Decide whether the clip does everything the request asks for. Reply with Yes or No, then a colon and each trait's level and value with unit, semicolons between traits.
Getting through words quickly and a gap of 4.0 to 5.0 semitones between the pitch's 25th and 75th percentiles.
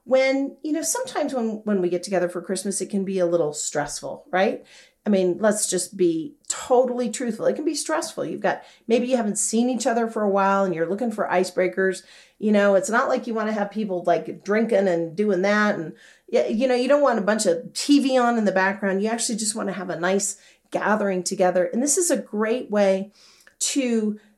Yes: fast, 225 wpm; average, 4.6 semitones